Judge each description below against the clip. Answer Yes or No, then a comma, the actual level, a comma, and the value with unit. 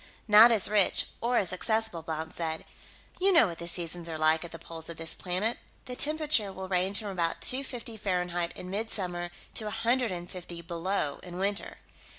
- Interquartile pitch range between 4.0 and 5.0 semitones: Yes, average, 4.4 semitones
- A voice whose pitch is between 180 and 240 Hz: Yes, medium, 185 Hz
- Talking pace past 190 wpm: Yes, average, 200 wpm